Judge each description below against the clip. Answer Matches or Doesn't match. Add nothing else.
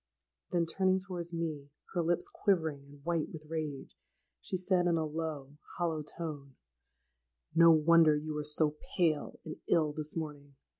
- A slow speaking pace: Doesn't match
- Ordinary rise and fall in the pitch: Doesn't match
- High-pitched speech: Doesn't match